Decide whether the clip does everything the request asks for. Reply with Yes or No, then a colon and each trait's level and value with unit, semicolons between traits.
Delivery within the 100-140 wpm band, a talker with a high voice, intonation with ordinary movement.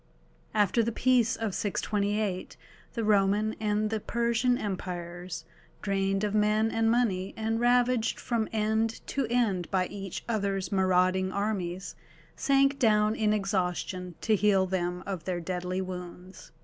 Yes: slow, 135 wpm; high, 205 Hz; average, 3.2 semitones